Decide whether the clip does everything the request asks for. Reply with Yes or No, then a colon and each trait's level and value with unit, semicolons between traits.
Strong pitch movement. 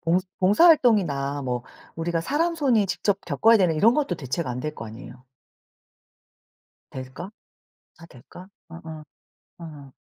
Yes: wide, 6.6 semitones